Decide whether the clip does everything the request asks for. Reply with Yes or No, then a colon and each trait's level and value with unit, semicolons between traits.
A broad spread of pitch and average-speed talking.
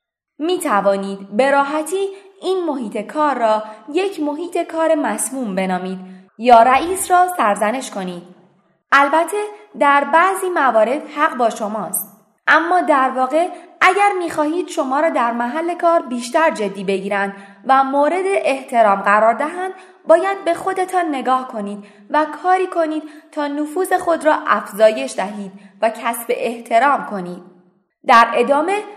Yes: wide, 7.8 semitones; average, 135 wpm